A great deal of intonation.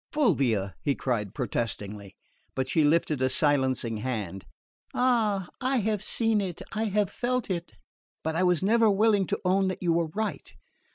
Yes: wide, 8.4 semitones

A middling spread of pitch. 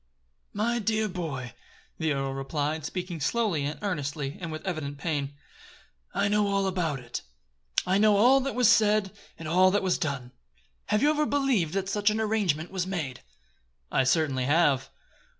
No: wide, 6.3 semitones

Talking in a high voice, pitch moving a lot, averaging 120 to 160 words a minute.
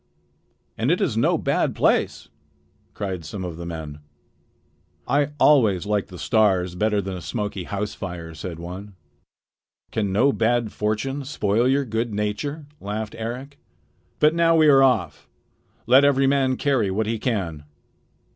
No: low, 105 Hz; wide, 5.9 semitones; average, 150 wpm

